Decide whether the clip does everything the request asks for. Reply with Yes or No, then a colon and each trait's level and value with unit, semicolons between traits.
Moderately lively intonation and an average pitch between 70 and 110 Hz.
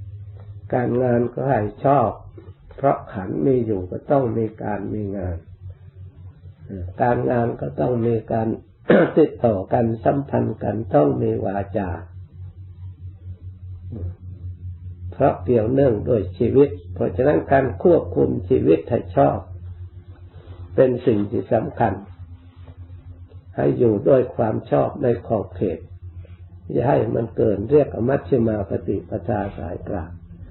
Yes: average, 3.9 semitones; very low, 95 Hz